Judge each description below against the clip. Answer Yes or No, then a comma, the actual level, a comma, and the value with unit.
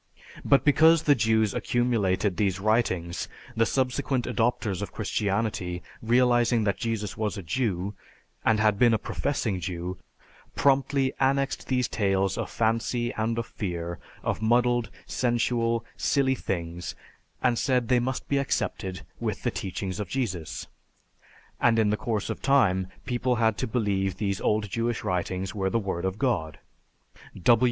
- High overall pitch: No, low, 110 Hz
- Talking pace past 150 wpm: No, average, 145 wpm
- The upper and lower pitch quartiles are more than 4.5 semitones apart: No, average, 4.2 semitones